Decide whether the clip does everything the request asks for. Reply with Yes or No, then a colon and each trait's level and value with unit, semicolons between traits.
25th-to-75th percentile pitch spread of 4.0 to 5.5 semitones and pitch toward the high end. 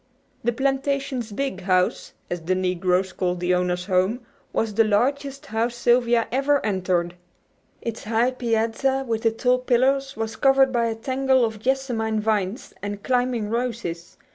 Yes: average, 4.3 semitones; high, 230 Hz